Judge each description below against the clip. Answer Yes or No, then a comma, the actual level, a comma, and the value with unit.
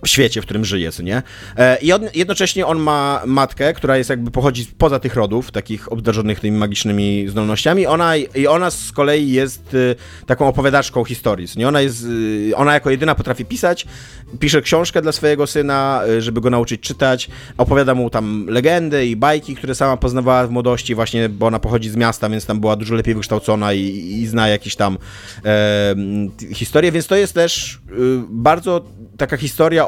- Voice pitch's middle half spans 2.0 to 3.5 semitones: No, average, 4.7 semitones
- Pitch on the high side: No, low, 125 Hz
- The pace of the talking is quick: Yes, fast, 180 wpm